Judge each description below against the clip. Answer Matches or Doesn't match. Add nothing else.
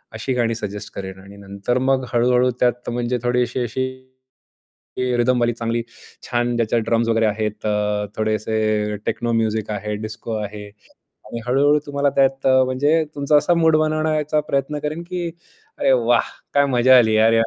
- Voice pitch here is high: Doesn't match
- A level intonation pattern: Doesn't match